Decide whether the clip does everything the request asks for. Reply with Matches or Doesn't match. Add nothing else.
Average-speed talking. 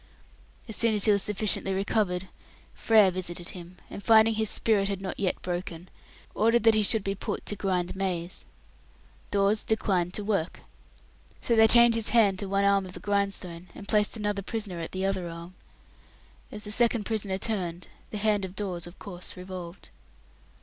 Matches